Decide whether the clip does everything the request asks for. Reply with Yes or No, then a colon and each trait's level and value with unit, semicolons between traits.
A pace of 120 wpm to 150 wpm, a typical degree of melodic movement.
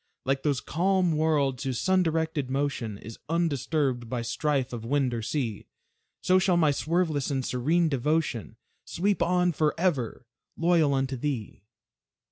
Yes: average, 140 wpm; average, 4.4 semitones